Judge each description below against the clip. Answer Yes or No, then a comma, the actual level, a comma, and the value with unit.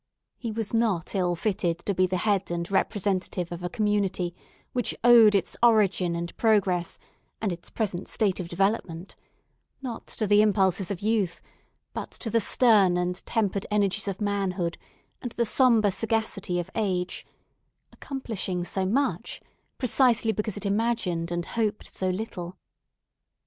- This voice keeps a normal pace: Yes, average, 150 wpm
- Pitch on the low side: No, high, 200 Hz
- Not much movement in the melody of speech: No, average, 3.6 semitones